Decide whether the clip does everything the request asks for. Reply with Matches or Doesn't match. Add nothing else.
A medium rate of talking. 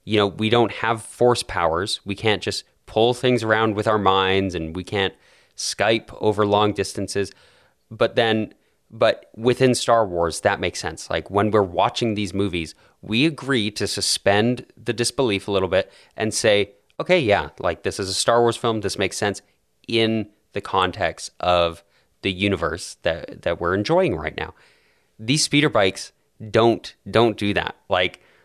Matches